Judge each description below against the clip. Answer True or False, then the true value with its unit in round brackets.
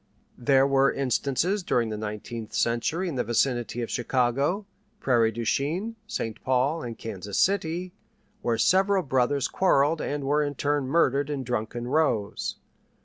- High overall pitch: False (135 Hz)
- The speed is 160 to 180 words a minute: False (145 wpm)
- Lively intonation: False (4.8 semitones)